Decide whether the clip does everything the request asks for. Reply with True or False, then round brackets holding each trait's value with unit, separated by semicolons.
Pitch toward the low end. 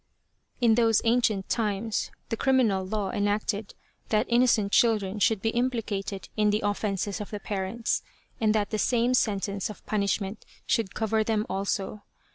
False (215 Hz)